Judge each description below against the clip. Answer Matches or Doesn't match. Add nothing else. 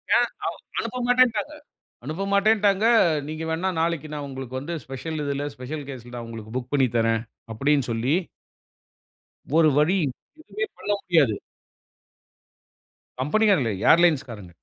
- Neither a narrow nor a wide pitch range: Doesn't match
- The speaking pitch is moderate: Matches